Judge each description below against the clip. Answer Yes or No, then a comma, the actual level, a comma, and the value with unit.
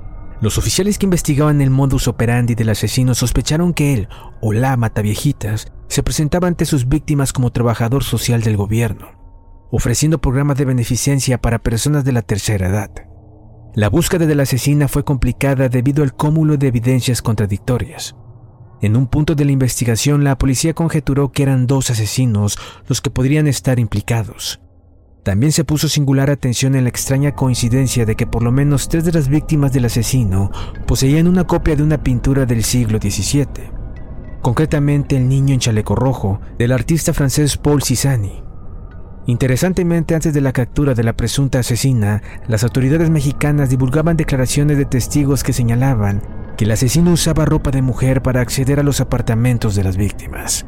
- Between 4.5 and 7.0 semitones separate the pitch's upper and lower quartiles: No, average, 4.0 semitones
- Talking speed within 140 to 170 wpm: Yes, average, 165 wpm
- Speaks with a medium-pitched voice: No, low, 130 Hz